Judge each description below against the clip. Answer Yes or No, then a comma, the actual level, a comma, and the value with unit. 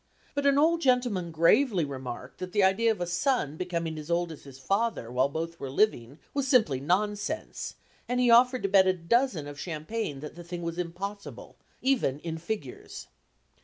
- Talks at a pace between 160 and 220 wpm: Yes, average, 185 wpm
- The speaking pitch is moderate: Yes, medium, 180 Hz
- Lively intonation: Yes, wide, 6.6 semitones